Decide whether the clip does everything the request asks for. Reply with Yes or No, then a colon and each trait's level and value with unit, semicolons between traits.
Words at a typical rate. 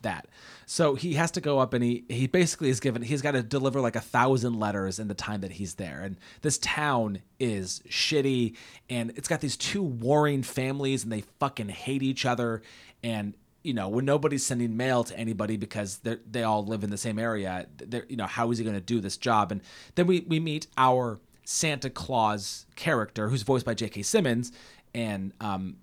No: fast, 210 wpm